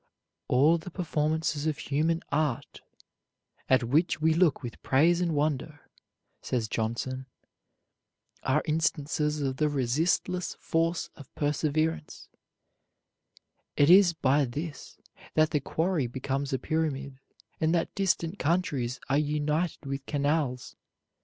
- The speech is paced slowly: Yes, slow, 120 wpm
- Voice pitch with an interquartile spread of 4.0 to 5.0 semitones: No, average, 2.9 semitones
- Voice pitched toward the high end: No, medium, 150 Hz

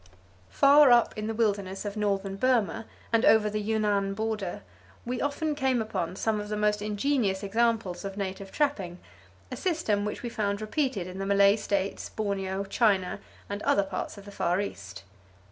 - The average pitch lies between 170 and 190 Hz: No, high, 210 Hz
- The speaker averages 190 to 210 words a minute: No, average, 175 wpm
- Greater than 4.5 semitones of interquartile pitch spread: No, narrow, 2.4 semitones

